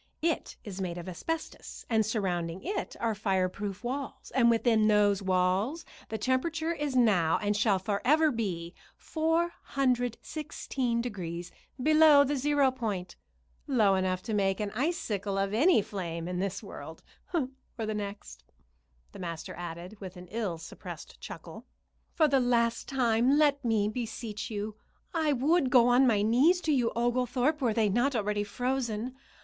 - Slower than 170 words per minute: Yes, average, 150 wpm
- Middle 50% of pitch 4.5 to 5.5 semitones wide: Yes, average, 5.1 semitones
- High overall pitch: Yes, high, 225 Hz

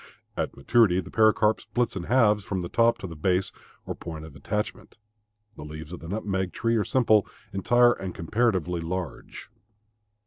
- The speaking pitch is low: Yes, very low, 95 Hz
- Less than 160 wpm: No, average, 170 wpm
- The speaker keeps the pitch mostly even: No, average, 4.3 semitones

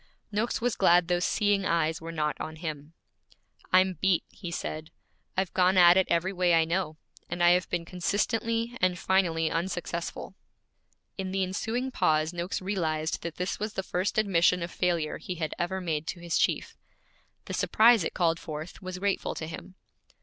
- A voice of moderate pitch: Yes, medium, 180 Hz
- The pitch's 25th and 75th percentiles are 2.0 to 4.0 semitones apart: Yes, narrow, 2.4 semitones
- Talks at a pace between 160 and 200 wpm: Yes, average, 180 wpm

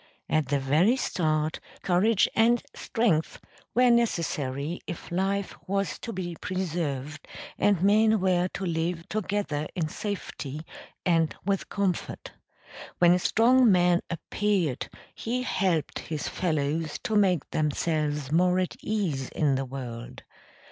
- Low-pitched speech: No, medium, 175 Hz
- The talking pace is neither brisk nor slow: No, slow, 125 wpm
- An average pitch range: Yes, average, 4.6 semitones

